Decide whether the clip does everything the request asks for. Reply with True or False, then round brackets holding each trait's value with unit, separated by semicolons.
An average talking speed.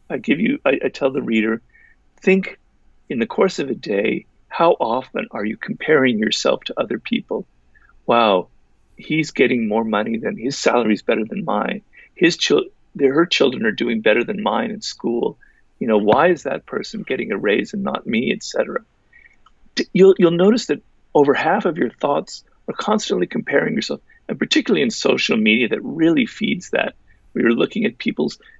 True (185 wpm)